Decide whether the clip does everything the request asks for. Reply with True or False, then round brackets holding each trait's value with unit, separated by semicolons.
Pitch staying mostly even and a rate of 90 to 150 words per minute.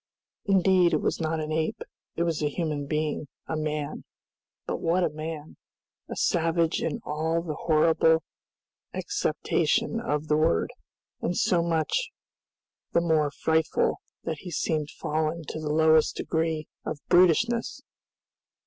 True (1.7 semitones; 140 wpm)